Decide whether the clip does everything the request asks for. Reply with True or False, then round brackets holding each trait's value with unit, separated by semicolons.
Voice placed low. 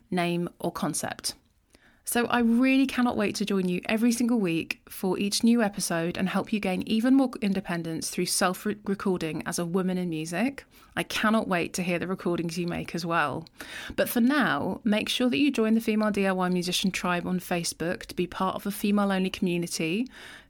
False (190 Hz)